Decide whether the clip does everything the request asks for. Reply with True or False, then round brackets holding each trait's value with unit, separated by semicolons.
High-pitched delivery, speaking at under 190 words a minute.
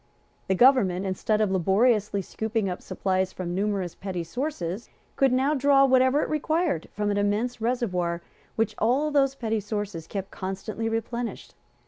True (215 Hz; 150 wpm)